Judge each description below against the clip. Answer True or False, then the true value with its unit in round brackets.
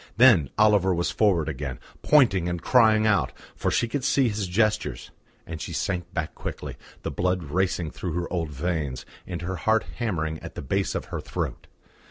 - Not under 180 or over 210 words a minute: True (185 wpm)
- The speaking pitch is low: True (90 Hz)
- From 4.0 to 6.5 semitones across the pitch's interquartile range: True (5.0 semitones)